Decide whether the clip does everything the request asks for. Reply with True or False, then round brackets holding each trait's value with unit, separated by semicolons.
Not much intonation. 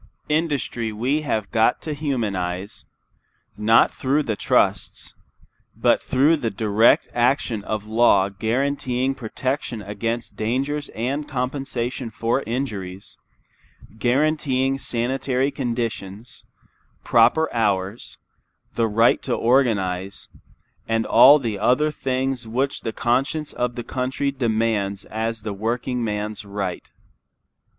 False (3.7 semitones)